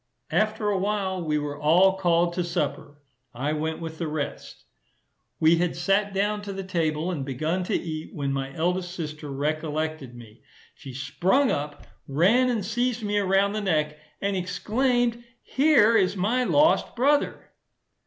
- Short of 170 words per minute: Yes, average, 160 wpm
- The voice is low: No, medium, 180 Hz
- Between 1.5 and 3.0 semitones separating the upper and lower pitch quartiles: No, average, 5.2 semitones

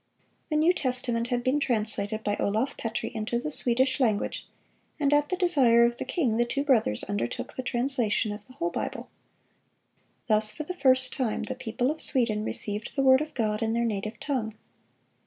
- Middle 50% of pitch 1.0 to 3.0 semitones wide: No, average, 3.8 semitones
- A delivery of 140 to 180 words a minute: No, average, 190 wpm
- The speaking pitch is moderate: No, high, 240 Hz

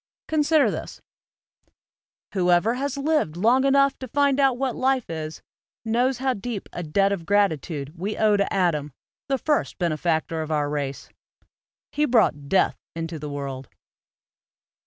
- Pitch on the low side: No, high, 200 Hz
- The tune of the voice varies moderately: No, wide, 8.9 semitones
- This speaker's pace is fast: No, average, 155 wpm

